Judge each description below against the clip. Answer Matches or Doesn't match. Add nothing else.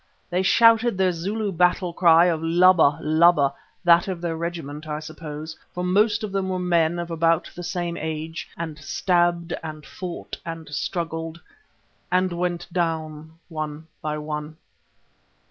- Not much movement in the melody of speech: Matches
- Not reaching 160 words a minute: Matches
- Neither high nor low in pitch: Matches